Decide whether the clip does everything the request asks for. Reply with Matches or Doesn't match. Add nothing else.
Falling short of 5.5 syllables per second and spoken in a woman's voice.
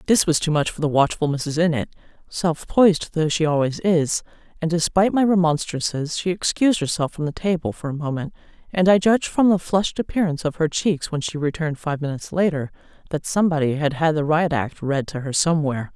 Doesn't match